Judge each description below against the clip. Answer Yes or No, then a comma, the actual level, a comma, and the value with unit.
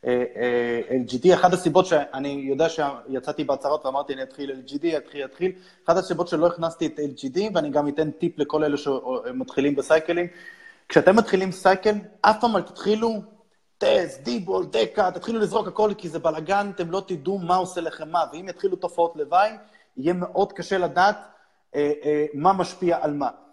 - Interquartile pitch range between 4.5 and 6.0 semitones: Yes, average, 4.8 semitones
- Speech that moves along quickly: Yes, fast, 155 wpm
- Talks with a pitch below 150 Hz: No, medium, 175 Hz